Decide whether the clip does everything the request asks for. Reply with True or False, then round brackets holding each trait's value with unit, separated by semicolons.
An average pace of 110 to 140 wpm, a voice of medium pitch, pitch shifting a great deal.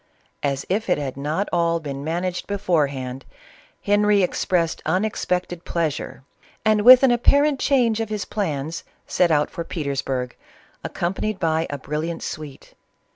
True (135 wpm; 170 Hz; 5.8 semitones)